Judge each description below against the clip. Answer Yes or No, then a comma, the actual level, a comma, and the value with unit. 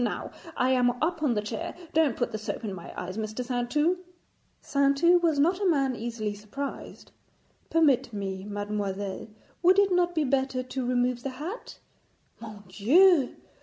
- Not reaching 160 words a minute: No, average, 165 wpm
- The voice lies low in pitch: No, very high, 255 Hz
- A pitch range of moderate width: No, wide, 6.7 semitones